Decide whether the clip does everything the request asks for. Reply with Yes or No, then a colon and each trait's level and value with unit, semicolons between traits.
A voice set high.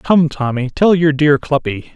No: medium, 145 Hz